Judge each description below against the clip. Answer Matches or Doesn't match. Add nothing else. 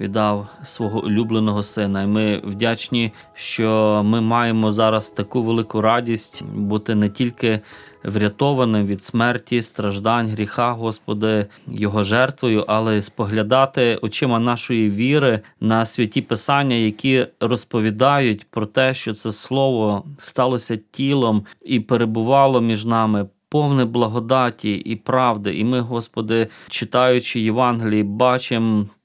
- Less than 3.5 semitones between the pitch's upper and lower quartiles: Matches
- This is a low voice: Matches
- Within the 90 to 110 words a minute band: Doesn't match